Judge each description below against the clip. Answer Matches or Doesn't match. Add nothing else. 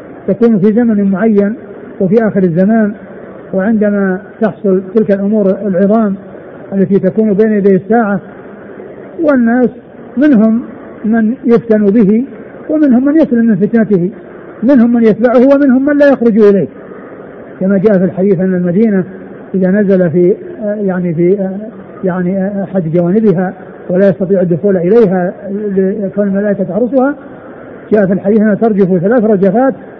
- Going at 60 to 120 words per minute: Doesn't match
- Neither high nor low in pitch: Doesn't match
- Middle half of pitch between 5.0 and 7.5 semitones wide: Doesn't match